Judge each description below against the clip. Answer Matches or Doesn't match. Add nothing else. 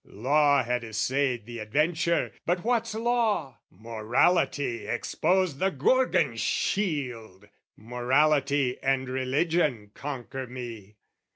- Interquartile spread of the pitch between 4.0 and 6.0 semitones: Matches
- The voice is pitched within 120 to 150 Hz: Matches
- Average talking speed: Doesn't match